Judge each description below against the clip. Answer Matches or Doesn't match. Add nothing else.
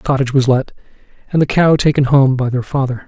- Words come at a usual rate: Doesn't match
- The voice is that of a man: Matches